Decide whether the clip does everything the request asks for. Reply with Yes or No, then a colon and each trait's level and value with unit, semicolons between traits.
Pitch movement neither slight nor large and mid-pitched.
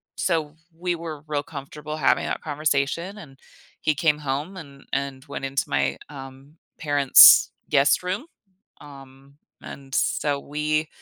No: narrow, 2.2 semitones; medium, 145 Hz